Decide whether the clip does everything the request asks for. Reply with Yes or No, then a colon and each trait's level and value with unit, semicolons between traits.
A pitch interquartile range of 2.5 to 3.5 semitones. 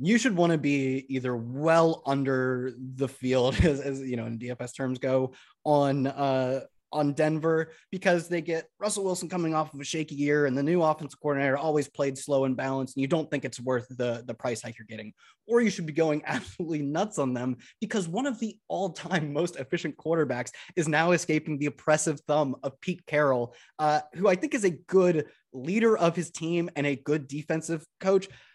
No: average, 4.1 semitones